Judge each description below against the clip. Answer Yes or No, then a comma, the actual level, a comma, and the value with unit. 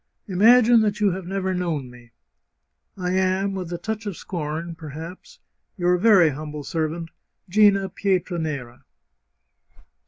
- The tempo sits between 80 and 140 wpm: Yes, slow, 135 wpm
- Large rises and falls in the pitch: No, average, 3.7 semitones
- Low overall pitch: No, medium, 180 Hz